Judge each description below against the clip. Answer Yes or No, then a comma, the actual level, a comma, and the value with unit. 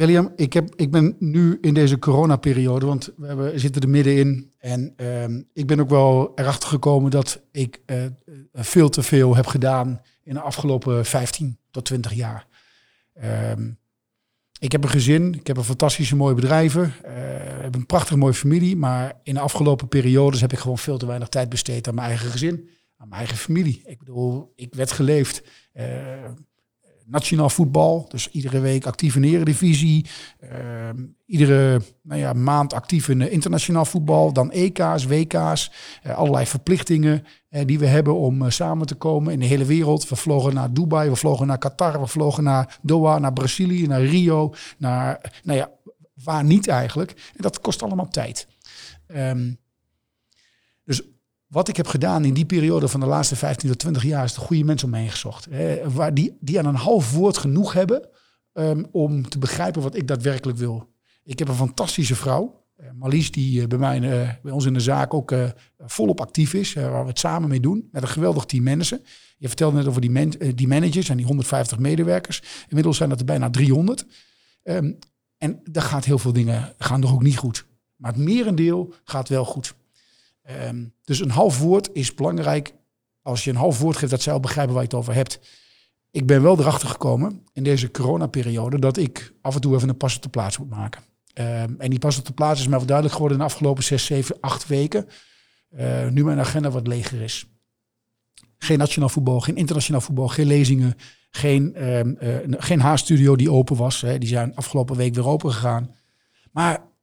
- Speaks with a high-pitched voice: No, low, 135 Hz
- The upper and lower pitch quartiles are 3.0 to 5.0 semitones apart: Yes, average, 3.3 semitones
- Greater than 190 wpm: Yes, fast, 200 wpm